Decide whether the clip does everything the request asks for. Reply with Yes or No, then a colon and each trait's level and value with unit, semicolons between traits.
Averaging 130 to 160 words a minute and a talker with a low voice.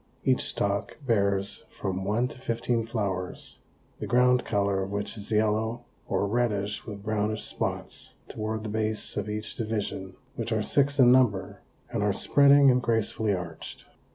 Yes: average, 155 wpm; low, 110 Hz